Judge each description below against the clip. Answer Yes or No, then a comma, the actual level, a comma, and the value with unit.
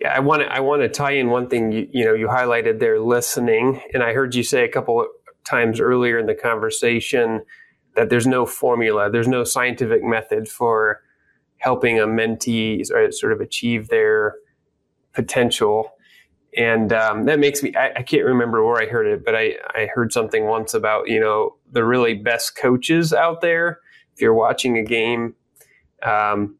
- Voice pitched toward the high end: No, low, 125 Hz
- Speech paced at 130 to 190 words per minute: Yes, average, 180 wpm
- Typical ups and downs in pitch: No, wide, 7.3 semitones